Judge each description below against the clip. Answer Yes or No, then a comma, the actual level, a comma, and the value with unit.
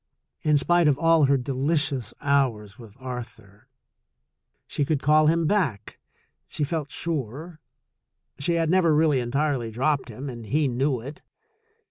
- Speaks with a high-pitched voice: No, medium, 140 Hz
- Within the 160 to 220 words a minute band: No, average, 140 wpm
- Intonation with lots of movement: No, average, 4.1 semitones